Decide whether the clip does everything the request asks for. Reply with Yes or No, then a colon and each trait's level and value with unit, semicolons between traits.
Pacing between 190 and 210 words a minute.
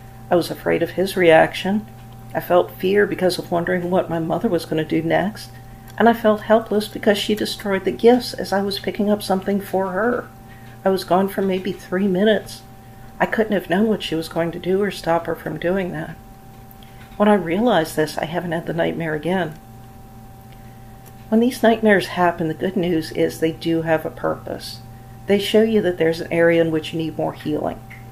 Yes: fast, 205 wpm